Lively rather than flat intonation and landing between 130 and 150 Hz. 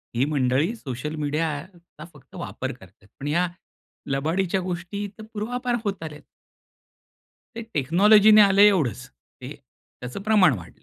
No: wide, 6.3 semitones; medium, 165 Hz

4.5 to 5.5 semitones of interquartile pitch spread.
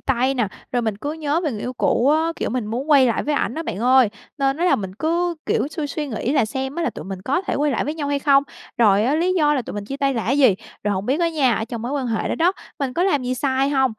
No: average, 4.0 semitones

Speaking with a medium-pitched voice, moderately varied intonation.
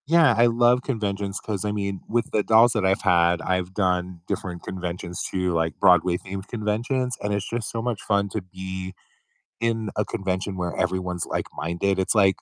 No: very low, 95 Hz; average, 3.3 semitones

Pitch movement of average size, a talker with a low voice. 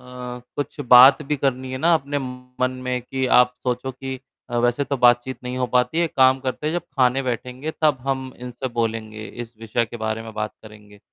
No: narrow, 1.7 semitones; low, 125 Hz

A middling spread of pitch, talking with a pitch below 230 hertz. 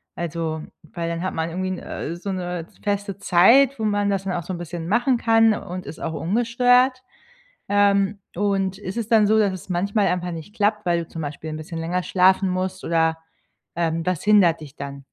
Yes: average, 3.5 semitones; medium, 185 Hz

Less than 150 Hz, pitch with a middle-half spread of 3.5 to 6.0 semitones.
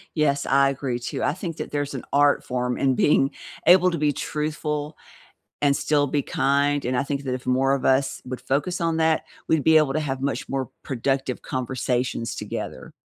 No: medium, 140 Hz; narrow, 2.4 semitones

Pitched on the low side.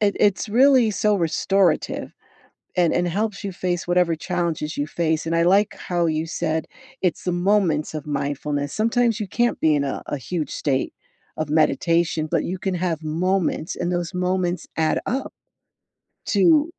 No: medium, 175 Hz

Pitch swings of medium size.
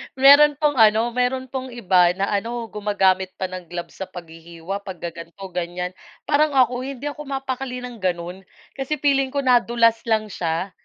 No: wide, 6.4 semitones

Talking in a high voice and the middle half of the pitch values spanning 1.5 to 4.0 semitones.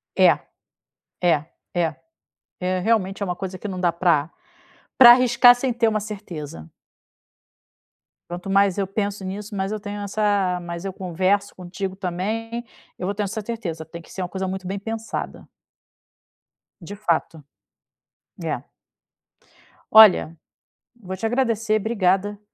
Yes: high, 195 Hz; average, 3.1 semitones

